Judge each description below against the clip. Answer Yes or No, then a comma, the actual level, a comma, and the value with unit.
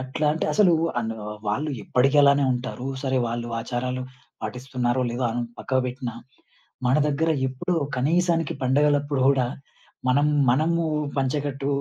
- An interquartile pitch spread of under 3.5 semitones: Yes, average, 2.9 semitones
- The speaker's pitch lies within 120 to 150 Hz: Yes, low, 135 Hz